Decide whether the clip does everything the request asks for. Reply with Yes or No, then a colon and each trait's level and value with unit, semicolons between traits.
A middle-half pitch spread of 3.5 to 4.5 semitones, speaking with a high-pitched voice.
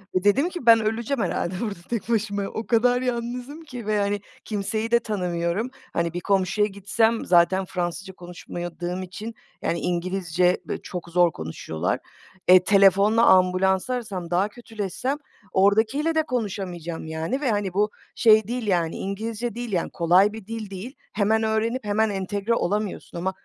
Yes: average, 3.8 semitones; high, 205 Hz